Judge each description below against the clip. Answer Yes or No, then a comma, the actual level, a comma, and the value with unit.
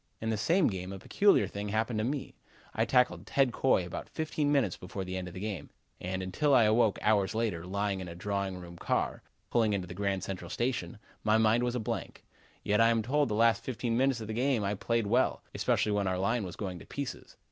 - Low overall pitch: Yes, low, 110 Hz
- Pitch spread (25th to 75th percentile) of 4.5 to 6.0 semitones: No, average, 4.0 semitones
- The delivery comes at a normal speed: No, fast, 235 wpm